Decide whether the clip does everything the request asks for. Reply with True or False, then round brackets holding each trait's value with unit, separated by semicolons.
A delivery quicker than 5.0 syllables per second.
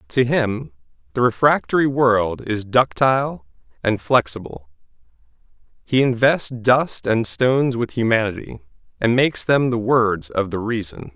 False (4.4 syllables/s)